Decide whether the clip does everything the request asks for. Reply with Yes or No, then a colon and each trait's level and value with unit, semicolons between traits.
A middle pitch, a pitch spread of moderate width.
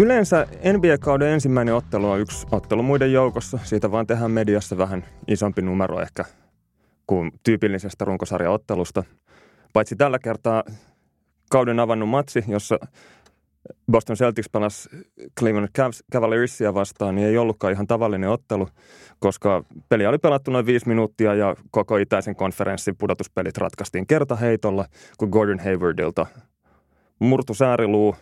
No: low, 110 Hz; average, 3.7 semitones